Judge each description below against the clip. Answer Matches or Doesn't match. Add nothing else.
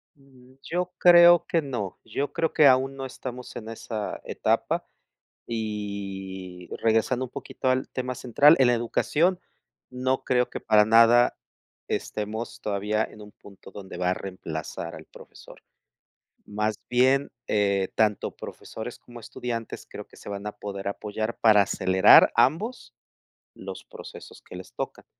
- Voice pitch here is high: Doesn't match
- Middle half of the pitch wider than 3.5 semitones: Matches